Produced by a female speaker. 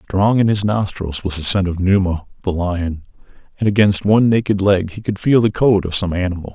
No: male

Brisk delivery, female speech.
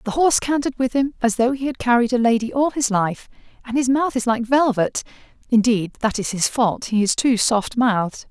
Yes: fast, 215 wpm; female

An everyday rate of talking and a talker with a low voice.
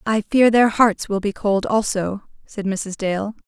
No: average, 190 wpm; high, 205 Hz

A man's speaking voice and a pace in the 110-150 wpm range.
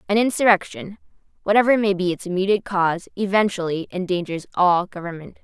No: female; slow, 135 wpm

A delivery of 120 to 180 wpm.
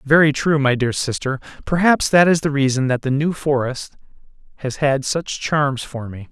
No: average, 190 wpm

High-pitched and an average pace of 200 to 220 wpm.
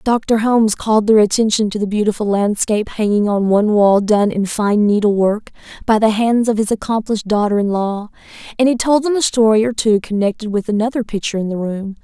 Yes: high, 215 Hz; fast, 205 wpm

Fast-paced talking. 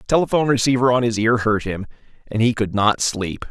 Yes: fast, 220 wpm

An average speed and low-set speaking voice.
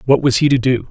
No: fast, 330 wpm; low, 130 Hz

